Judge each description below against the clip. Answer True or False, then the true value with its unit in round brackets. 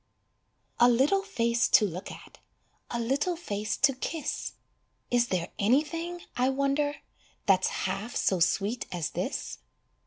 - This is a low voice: False (245 Hz)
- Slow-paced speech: True (130 wpm)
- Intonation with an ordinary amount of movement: False (6.0 semitones)